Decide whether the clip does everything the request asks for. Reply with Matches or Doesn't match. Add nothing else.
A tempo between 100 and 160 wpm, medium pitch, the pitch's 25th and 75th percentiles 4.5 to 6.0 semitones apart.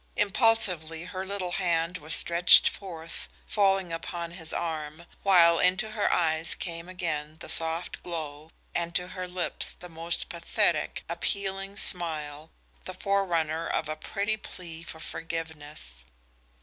Doesn't match